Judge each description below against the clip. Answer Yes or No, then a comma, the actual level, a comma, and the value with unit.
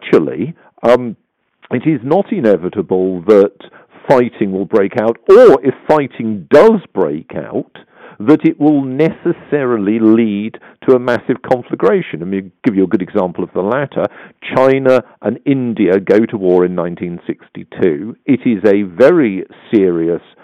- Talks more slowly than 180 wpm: Yes, average, 165 wpm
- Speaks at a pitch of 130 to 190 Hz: No, low, 115 Hz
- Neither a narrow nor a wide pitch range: No, wide, 6.3 semitones